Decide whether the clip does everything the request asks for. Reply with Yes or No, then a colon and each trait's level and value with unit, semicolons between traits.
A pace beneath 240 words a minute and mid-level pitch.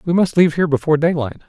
No: fast, 245 wpm; medium, 160 Hz